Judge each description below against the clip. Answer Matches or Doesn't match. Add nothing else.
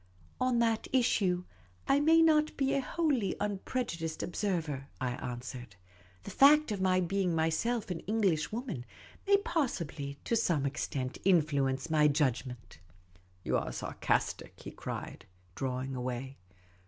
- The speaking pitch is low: Doesn't match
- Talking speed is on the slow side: Doesn't match